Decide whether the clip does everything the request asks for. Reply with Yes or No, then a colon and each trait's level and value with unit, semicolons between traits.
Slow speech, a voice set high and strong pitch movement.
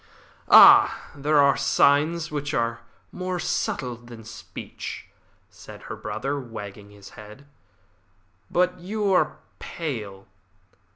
No: slow, 110 wpm; medium, 140 Hz; wide, 6.6 semitones